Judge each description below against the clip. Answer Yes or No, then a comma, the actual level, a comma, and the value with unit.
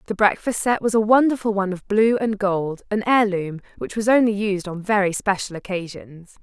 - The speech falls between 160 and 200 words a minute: Yes, average, 195 wpm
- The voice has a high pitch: Yes, high, 205 Hz